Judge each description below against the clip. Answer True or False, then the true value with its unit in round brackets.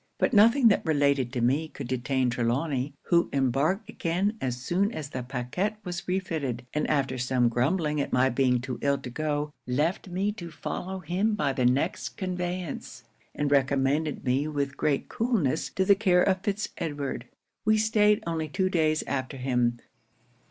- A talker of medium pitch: True (150 Hz)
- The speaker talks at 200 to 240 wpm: False (170 wpm)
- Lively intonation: True (5.8 semitones)